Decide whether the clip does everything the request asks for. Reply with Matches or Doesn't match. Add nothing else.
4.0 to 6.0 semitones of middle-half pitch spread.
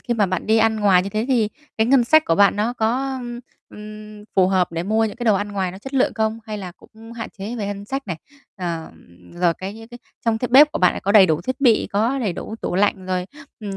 Doesn't match